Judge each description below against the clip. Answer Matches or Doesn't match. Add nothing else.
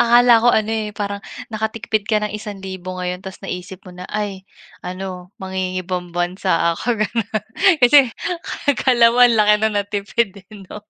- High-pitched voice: Matches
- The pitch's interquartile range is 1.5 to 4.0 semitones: Matches